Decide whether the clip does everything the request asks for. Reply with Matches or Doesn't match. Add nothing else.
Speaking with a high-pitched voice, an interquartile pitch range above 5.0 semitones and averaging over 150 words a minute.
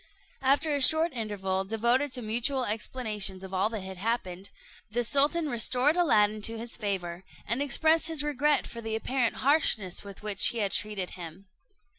Matches